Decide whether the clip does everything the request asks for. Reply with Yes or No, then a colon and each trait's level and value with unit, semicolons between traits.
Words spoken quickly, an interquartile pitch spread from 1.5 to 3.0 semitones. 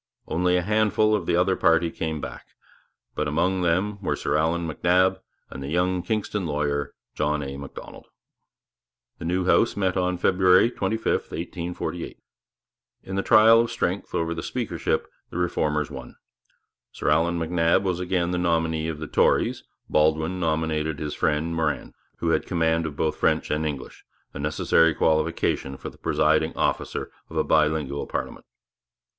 No: average, 160 wpm; average, 2.7 semitones